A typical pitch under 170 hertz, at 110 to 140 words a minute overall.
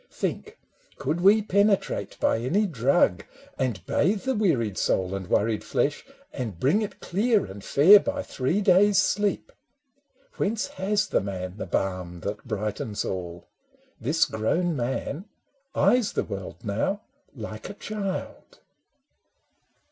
Yes: medium, 140 Hz; slow, 135 wpm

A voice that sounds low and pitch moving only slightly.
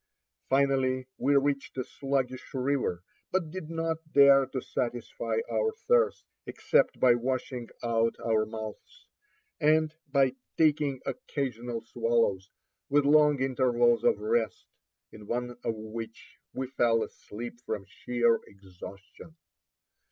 No: low, 130 Hz; average, 3.6 semitones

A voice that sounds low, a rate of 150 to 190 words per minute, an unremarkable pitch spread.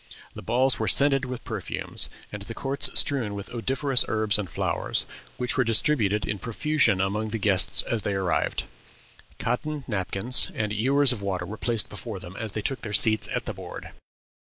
Yes: low, 110 Hz; average, 180 wpm; average, 4.1 semitones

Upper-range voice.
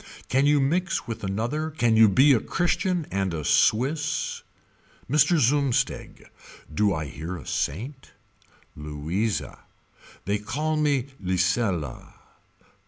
No: low, 115 Hz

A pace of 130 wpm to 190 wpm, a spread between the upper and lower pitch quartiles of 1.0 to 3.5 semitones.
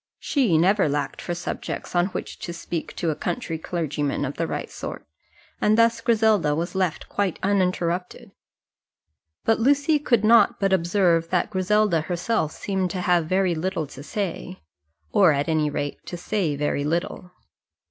No: average, 160 wpm; average, 3.9 semitones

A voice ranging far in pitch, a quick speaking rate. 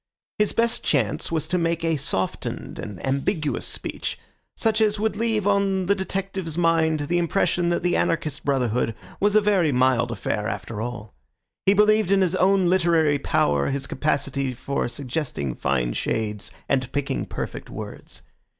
No: wide, 6.8 semitones; average, 160 wpm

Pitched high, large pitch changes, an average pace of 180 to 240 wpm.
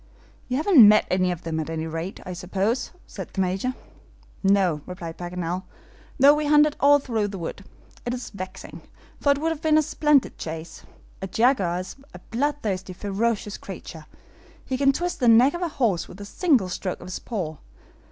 Yes: high, 205 Hz; wide, 7.2 semitones; average, 190 wpm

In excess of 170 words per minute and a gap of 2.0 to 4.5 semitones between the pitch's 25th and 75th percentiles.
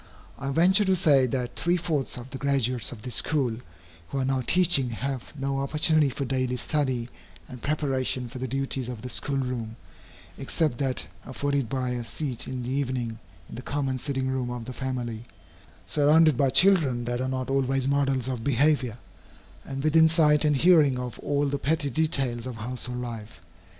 Yes: average, 180 wpm; narrow, 2.5 semitones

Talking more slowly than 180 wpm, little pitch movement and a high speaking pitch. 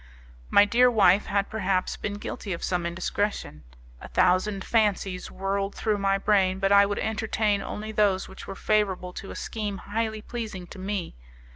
Yes: average, 170 wpm; narrow, 1.9 semitones; high, 200 Hz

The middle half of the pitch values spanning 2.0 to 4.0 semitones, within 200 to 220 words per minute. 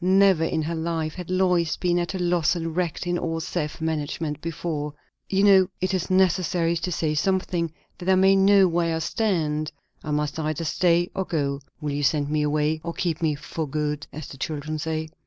Yes: average, 2.8 semitones; fast, 205 wpm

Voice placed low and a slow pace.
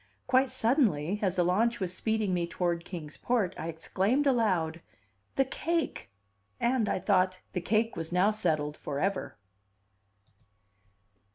No: high, 190 Hz; slow, 130 wpm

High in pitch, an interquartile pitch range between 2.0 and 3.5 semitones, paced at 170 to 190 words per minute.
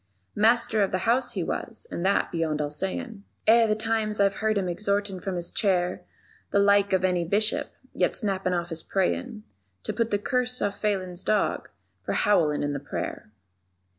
Yes: high, 200 Hz; average, 3.2 semitones; average, 185 wpm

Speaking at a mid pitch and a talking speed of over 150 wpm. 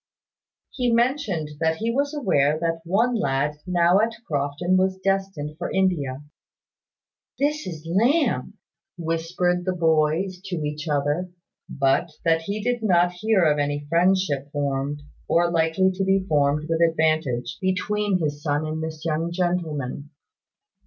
No: medium, 170 Hz; average, 140 wpm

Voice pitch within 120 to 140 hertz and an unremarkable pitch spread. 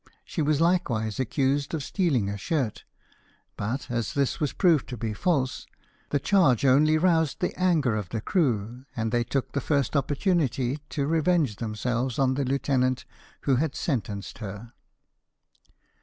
Yes: low, 135 Hz; average, 4.6 semitones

